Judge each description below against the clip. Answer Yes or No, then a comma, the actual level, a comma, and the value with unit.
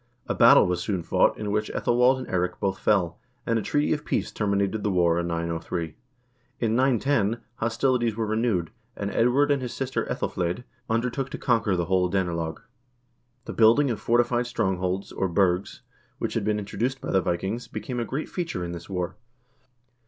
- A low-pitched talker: Yes, low, 105 Hz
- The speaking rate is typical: Yes, average, 180 wpm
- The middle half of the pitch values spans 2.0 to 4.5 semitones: No, average, 5.0 semitones